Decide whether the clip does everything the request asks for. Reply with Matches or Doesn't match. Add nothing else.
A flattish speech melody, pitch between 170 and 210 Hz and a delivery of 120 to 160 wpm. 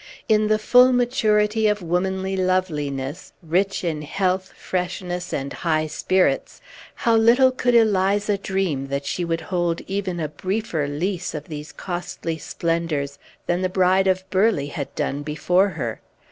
Doesn't match